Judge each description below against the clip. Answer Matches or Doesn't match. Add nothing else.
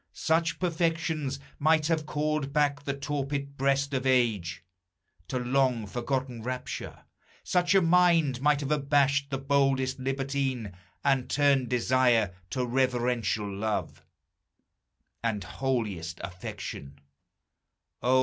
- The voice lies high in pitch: Doesn't match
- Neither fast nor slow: Doesn't match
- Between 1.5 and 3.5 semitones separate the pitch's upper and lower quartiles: Matches